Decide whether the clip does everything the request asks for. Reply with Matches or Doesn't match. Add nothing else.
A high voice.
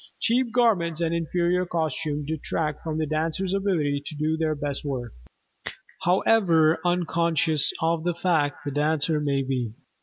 Doesn't match